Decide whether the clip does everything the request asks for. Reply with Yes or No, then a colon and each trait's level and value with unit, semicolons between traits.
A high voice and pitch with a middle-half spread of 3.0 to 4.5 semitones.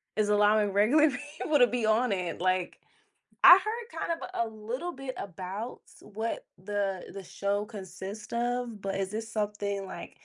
Yes: high, 210 Hz; average, 3.6 semitones